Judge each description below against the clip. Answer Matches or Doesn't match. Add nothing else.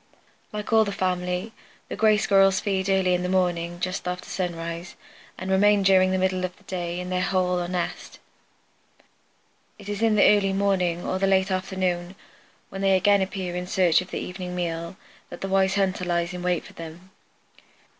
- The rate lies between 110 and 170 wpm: Doesn't match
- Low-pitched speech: Doesn't match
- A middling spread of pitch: Doesn't match